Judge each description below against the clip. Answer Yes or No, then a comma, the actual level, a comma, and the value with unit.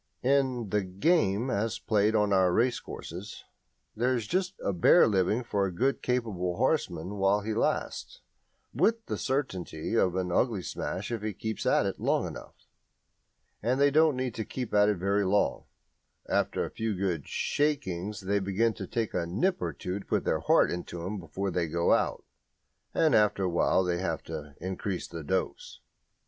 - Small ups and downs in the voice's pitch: No, average, 4.7 semitones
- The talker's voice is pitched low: Yes, low, 100 Hz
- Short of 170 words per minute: No, average, 180 wpm